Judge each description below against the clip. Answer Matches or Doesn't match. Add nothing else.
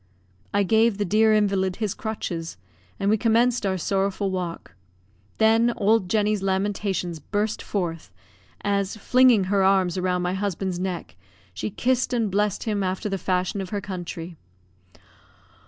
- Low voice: Doesn't match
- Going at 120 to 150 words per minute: Matches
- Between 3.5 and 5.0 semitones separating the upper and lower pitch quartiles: Doesn't match